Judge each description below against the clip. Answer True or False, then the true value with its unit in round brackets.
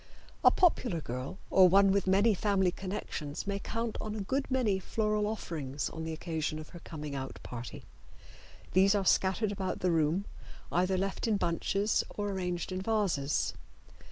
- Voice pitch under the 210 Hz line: True (190 Hz)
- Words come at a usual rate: True (165 wpm)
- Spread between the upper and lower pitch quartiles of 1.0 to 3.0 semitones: False (4.1 semitones)